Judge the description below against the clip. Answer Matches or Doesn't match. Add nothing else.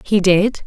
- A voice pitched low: Doesn't match